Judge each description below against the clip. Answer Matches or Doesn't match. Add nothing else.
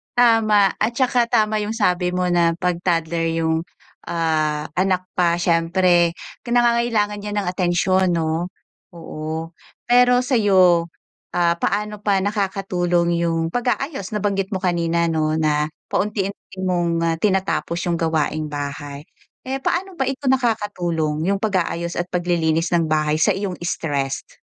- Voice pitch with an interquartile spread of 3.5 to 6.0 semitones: Matches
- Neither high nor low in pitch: Matches